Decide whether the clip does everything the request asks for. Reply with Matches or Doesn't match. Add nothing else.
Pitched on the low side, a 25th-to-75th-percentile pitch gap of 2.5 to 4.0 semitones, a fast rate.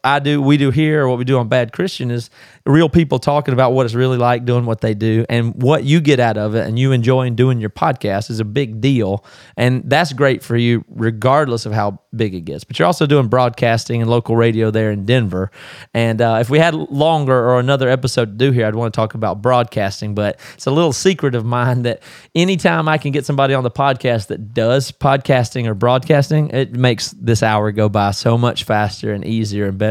Matches